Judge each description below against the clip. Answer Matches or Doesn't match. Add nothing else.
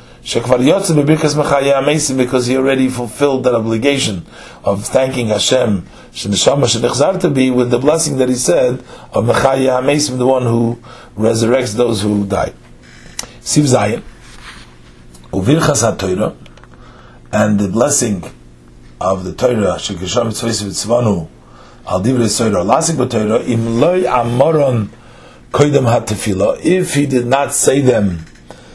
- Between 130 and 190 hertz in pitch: Doesn't match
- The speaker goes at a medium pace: Doesn't match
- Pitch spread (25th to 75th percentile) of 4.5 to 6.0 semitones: Matches